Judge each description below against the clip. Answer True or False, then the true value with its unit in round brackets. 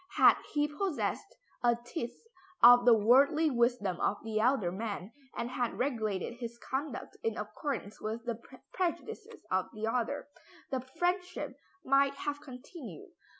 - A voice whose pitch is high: True (245 Hz)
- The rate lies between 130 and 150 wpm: True (140 wpm)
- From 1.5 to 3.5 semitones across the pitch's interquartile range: False (4.3 semitones)